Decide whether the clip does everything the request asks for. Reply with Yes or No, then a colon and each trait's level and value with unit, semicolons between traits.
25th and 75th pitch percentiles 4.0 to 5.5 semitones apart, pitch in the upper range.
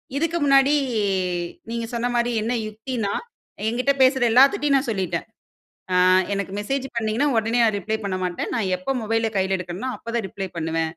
Yes: average, 5.1 semitones; high, 225 Hz